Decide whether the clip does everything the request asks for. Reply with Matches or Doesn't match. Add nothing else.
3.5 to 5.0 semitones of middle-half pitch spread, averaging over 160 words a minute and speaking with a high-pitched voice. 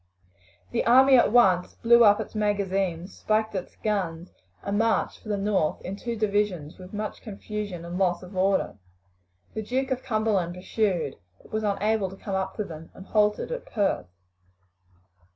Doesn't match